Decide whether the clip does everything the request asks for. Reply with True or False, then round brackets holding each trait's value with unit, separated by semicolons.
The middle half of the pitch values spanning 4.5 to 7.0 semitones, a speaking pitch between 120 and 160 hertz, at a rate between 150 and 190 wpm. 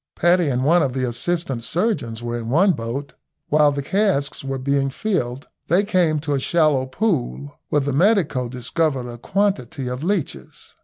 True (5.3 semitones; 140 Hz; 170 wpm)